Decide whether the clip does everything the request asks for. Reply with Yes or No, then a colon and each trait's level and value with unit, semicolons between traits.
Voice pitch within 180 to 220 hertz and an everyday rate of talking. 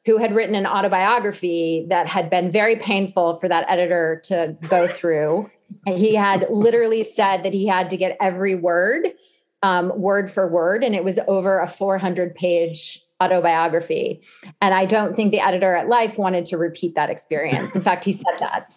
Yes: high, 190 Hz; average, 185 wpm